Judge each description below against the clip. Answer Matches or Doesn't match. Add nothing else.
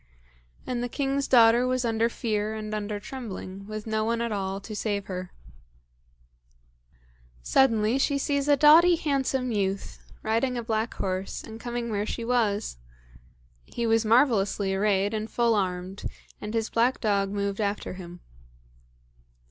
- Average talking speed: Matches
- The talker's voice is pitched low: Doesn't match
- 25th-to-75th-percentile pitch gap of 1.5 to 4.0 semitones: Matches